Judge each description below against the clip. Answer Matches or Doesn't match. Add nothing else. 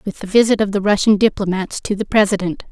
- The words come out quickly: Matches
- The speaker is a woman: Matches